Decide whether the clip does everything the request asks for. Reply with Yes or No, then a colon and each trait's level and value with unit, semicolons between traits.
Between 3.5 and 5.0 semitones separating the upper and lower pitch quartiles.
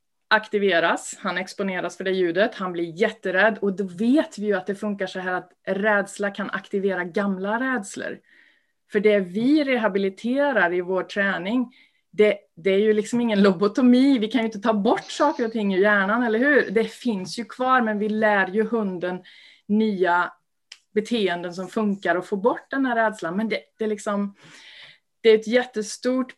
No: average, 2.8 semitones